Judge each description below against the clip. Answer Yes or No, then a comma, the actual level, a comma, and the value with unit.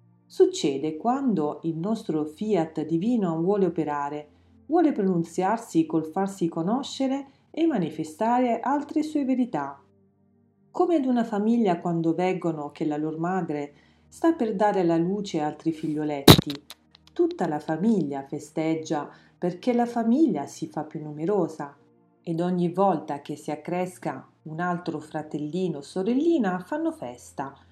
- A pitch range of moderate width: No, wide, 6.8 semitones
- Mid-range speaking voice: Yes, medium, 170 Hz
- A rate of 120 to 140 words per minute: Yes, average, 130 wpm